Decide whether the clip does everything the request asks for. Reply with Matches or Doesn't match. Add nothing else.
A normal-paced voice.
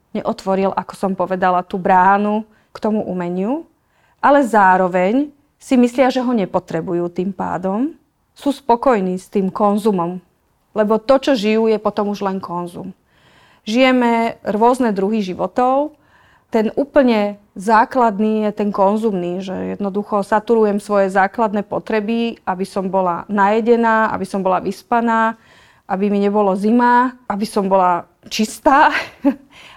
Matches